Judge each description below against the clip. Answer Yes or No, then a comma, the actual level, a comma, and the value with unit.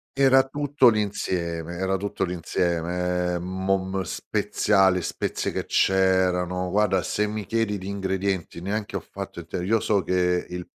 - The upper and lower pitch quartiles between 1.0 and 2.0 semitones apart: No, narrow, 2.4 semitones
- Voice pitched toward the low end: Yes, very low, 95 Hz